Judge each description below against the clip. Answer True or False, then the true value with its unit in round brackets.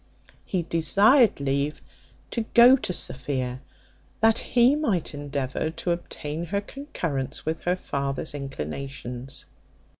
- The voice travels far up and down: True (6.8 semitones)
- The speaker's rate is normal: False (115 wpm)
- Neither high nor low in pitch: True (155 Hz)